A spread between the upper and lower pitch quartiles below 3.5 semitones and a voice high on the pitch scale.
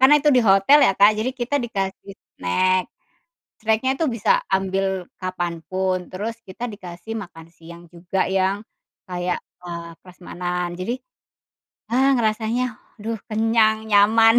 No: average, 3.8 semitones; high, 195 Hz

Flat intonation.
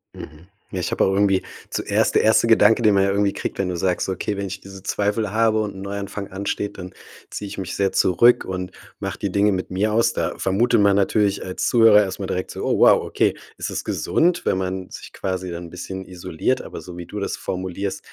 Yes: narrow, 2.0 semitones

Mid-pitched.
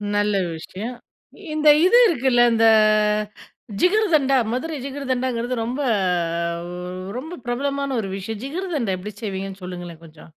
No: high, 245 Hz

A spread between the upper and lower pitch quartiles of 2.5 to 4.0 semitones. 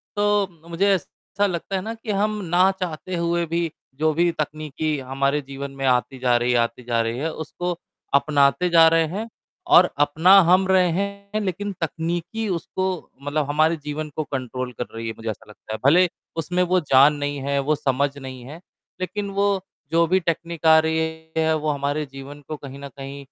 No: average, 4.5 semitones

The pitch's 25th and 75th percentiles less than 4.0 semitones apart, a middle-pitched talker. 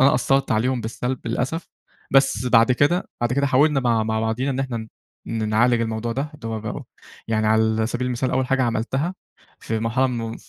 No: average, 2.9 semitones; low, 120 Hz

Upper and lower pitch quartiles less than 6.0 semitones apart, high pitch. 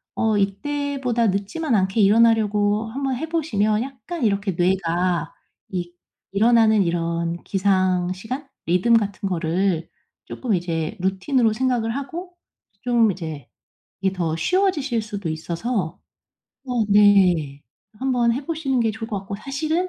Yes: average, 5.3 semitones; high, 210 Hz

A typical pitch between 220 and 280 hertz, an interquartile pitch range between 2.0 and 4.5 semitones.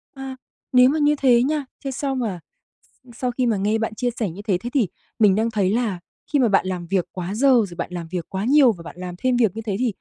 No: high, 225 Hz; average, 5.0 semitones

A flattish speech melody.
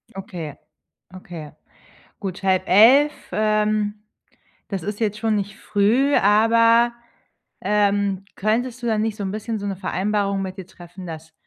Yes: narrow, 2.3 semitones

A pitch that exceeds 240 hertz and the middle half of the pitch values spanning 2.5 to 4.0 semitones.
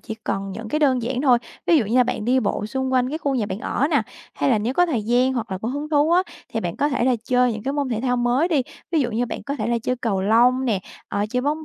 Yes: very high, 250 Hz; average, 3.6 semitones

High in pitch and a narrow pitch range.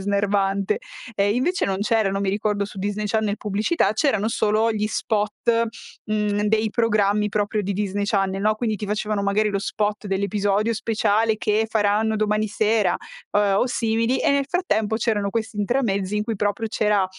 Yes: high, 210 Hz; narrow, 1.5 semitones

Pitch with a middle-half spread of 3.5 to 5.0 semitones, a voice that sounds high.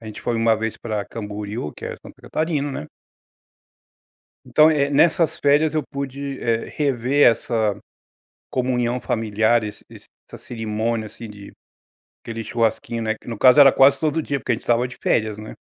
No: average, 4.0 semitones; low, 120 Hz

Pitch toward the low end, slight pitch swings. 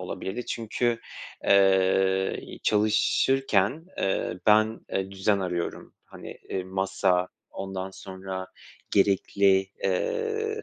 Yes: very low, 95 Hz; narrow, 2.3 semitones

